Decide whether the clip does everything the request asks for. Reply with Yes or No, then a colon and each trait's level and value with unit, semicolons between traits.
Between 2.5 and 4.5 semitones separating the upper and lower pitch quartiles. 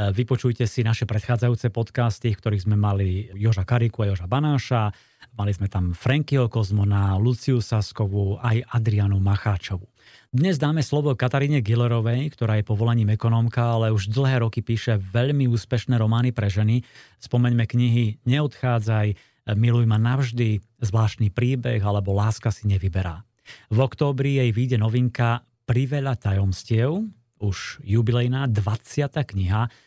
Yes: average, 2.8 semitones